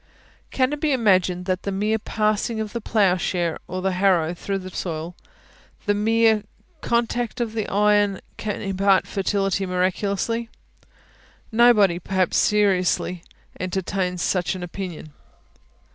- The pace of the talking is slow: Yes, slow, 130 wpm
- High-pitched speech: Yes, high, 195 Hz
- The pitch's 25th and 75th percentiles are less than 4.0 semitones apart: Yes, average, 2.8 semitones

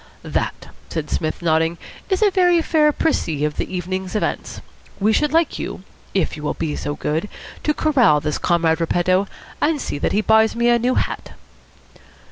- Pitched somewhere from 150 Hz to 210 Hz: Yes, high, 190 Hz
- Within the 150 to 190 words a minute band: Yes, average, 180 wpm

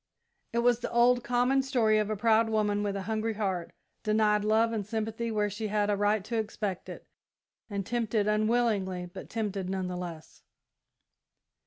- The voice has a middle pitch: No, high, 215 Hz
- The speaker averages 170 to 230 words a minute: Yes, average, 175 wpm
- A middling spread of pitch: No, narrow, 2.0 semitones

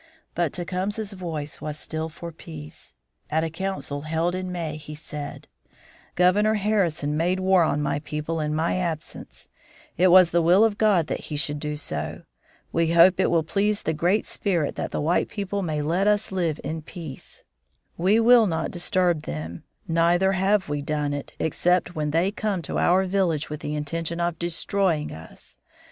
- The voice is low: No, medium, 170 Hz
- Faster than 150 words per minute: Yes, average, 180 wpm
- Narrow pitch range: No, average, 3.6 semitones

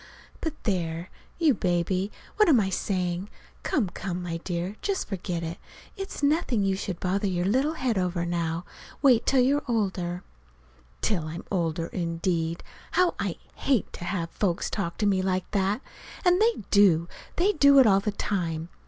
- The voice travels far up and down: Yes, wide, 5.8 semitones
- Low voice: No, high, 190 Hz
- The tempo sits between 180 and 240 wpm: No, average, 170 wpm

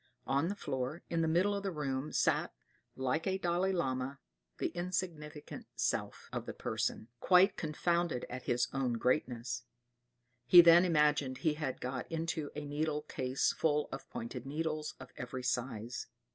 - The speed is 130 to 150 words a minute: No, average, 160 wpm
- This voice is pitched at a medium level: Yes, medium, 150 Hz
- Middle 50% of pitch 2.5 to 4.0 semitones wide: No, average, 4.7 semitones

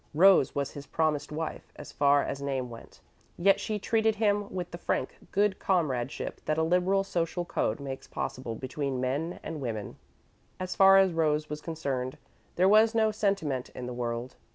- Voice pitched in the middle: Yes, medium, 155 Hz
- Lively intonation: Yes, wide, 6.4 semitones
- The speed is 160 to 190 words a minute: Yes, average, 175 wpm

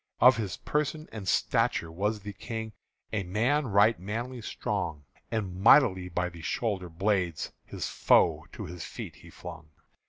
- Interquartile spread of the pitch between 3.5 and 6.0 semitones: Yes, average, 4.4 semitones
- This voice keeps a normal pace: Yes, average, 150 wpm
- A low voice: Yes, low, 100 Hz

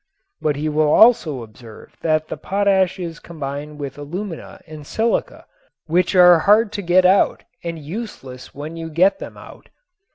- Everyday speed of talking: Yes, average, 160 wpm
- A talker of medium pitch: Yes, medium, 165 Hz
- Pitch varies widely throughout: No, average, 4.1 semitones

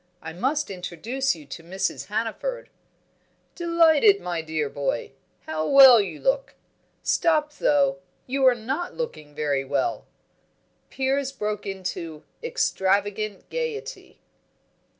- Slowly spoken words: Yes, slow, 115 wpm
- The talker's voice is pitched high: Yes, high, 220 Hz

